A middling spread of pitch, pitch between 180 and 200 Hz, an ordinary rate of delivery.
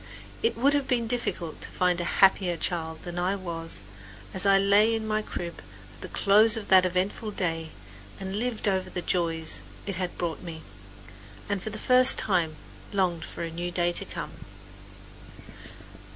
Yes: average, 3.6 semitones; medium, 185 Hz; average, 175 wpm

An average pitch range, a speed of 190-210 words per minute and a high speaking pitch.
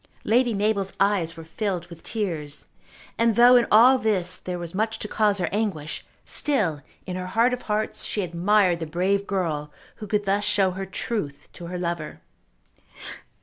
No: average, 3.8 semitones; average, 175 wpm; high, 195 Hz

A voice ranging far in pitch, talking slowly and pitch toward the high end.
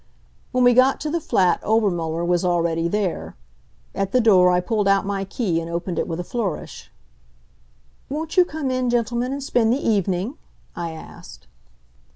No: wide, 5.9 semitones; average, 175 wpm; high, 200 Hz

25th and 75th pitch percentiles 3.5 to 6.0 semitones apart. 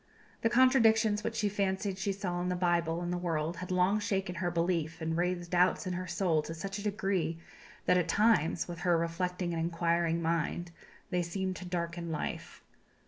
No: narrow, 2.4 semitones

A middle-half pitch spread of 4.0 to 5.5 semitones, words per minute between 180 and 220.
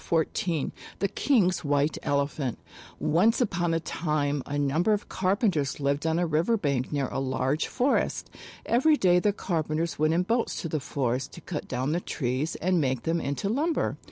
Yes: average, 4.6 semitones; average, 185 wpm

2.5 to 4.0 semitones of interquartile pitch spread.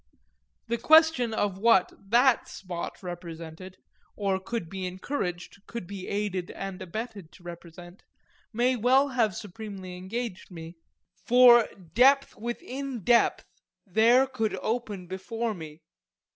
No: average, 4.7 semitones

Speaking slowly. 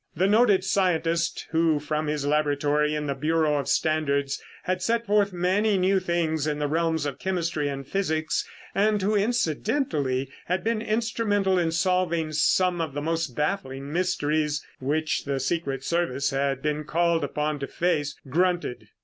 No: average, 160 wpm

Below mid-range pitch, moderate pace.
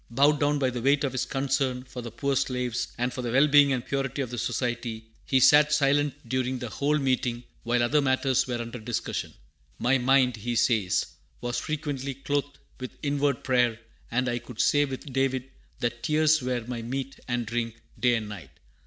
Yes: low, 130 Hz; average, 195 wpm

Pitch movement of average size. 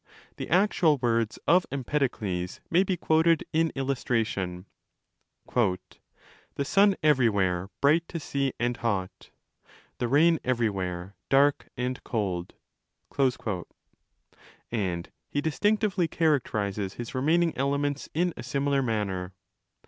No: wide, 7.4 semitones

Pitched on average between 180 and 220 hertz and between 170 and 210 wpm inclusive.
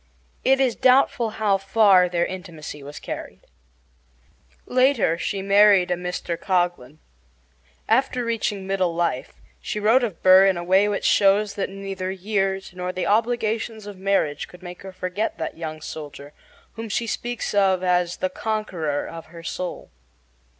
No: high, 190 Hz; average, 155 wpm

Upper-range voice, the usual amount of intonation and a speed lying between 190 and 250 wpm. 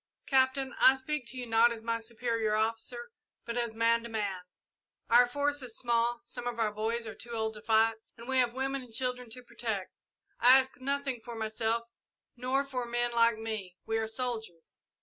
No: high, 235 Hz; narrow, 2.1 semitones; average, 195 wpm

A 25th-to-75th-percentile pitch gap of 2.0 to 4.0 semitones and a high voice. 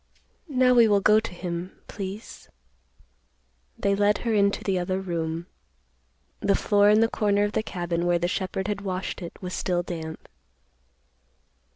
Yes: average, 2.9 semitones; high, 195 Hz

